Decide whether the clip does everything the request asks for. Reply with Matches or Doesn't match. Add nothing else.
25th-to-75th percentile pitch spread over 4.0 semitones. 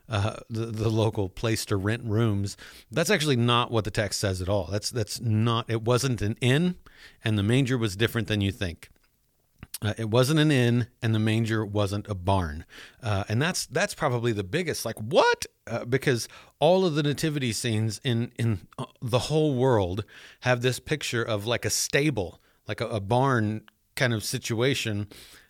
Doesn't match